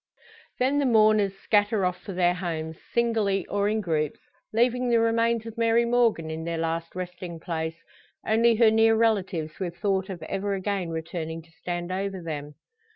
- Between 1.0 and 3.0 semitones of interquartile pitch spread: No, average, 5.1 semitones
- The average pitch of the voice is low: No, high, 195 Hz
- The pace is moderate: Yes, average, 170 wpm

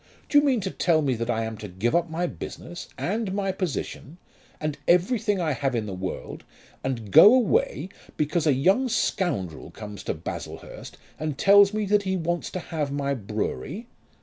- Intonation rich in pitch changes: Yes, wide, 8.2 semitones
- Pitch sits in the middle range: Yes, medium, 165 Hz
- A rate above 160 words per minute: Yes, average, 185 wpm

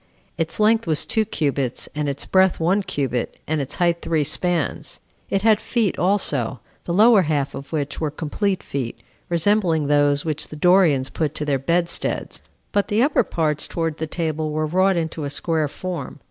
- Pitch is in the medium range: Yes, medium, 160 Hz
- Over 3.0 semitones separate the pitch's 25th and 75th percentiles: Yes, average, 4.2 semitones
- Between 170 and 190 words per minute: Yes, average, 180 wpm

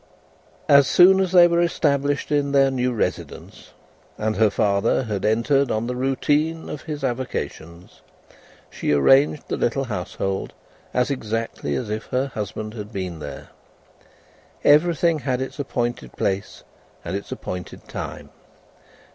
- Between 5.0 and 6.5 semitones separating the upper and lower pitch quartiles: Yes, average, 5.3 semitones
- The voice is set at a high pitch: No, low, 125 Hz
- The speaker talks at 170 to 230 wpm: No, average, 140 wpm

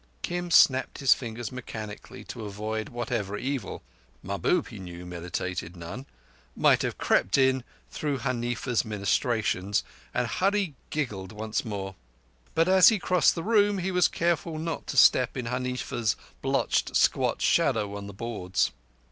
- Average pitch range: No, wide, 6.4 semitones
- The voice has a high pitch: No, low, 115 Hz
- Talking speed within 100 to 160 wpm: Yes, average, 140 wpm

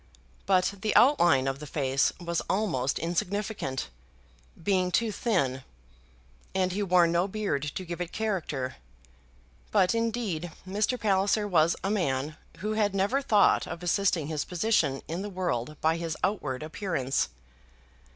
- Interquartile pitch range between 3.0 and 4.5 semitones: No, average, 4.9 semitones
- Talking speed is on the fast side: No, average, 140 wpm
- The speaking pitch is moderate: Yes, medium, 180 Hz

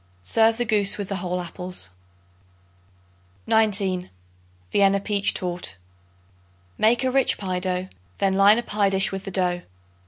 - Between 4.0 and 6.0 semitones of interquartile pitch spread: No, narrow, 2.6 semitones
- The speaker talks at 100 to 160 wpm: Yes, average, 145 wpm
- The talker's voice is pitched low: No, high, 195 Hz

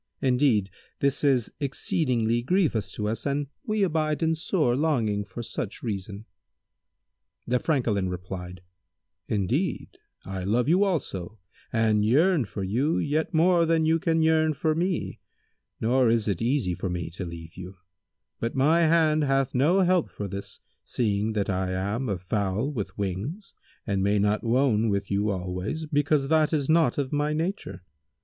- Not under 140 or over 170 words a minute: Yes, average, 160 wpm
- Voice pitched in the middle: No, low, 125 Hz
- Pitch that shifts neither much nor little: No, wide, 7.6 semitones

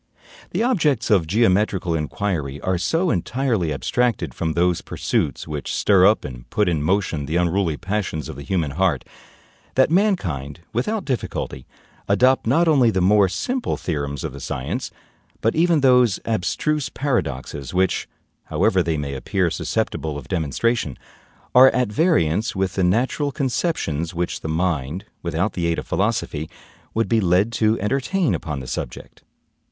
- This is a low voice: Yes, very low, 95 Hz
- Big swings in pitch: Yes, wide, 7.4 semitones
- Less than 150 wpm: No, average, 155 wpm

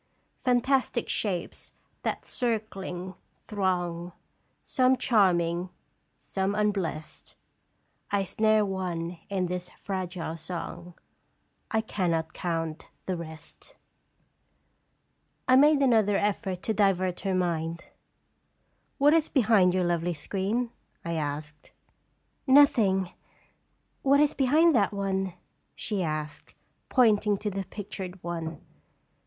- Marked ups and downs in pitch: No, average, 3.9 semitones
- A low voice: No, high, 190 Hz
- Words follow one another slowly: Yes, slow, 115 wpm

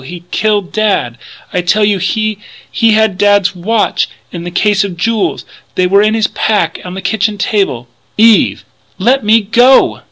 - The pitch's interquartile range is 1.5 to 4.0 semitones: Yes, average, 3.0 semitones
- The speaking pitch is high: Yes, high, 205 Hz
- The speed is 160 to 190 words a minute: Yes, average, 170 wpm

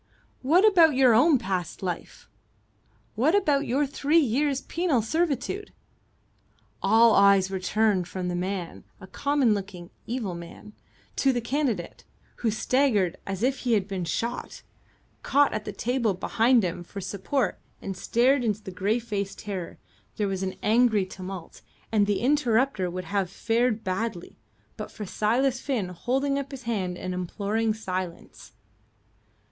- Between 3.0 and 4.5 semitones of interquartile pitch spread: No, wide, 5.6 semitones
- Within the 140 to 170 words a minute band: Yes, average, 145 wpm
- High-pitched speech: Yes, high, 220 Hz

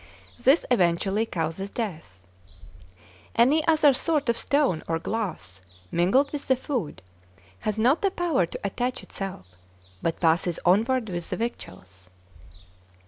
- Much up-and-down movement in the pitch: Yes, wide, 7.6 semitones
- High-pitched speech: Yes, high, 215 Hz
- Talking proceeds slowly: Yes, slow, 130 wpm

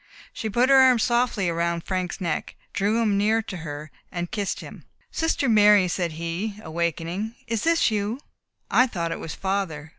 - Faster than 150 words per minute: Yes, average, 175 wpm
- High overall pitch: Yes, high, 200 Hz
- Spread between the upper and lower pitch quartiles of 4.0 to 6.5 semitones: Yes, average, 4.8 semitones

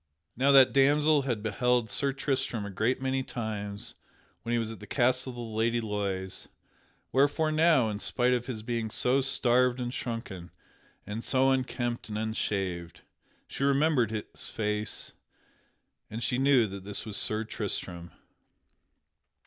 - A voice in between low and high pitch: No, low, 120 Hz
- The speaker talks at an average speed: Yes, average, 150 wpm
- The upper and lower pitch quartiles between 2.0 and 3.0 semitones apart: No, average, 3.7 semitones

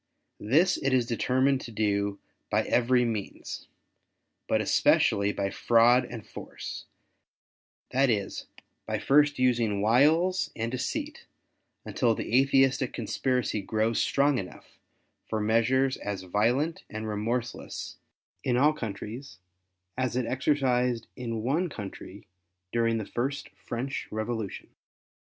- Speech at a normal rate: No, slow, 120 wpm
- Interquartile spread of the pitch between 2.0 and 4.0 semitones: Yes, average, 3.5 semitones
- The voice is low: Yes, low, 120 Hz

